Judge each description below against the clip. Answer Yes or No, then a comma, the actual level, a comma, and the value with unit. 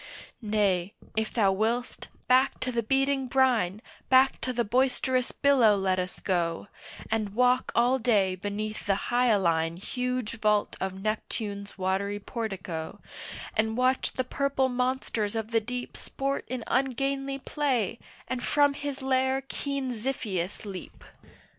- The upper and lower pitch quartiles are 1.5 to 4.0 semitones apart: No, average, 4.4 semitones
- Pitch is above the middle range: Yes, high, 230 Hz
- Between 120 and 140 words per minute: Yes, slow, 135 wpm